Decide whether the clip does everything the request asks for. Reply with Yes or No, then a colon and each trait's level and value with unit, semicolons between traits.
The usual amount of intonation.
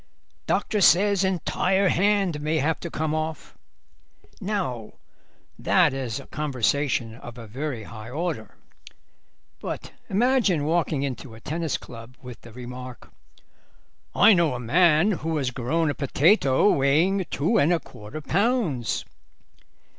No: wide, 6.1 semitones